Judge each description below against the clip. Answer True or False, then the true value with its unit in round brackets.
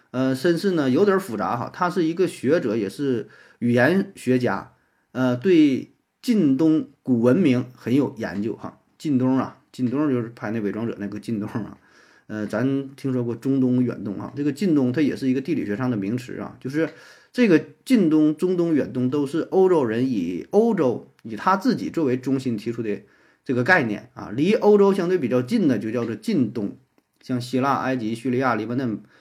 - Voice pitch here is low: True (130 Hz)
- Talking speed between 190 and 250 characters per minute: False (280 characters per minute)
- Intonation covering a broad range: True (6.2 semitones)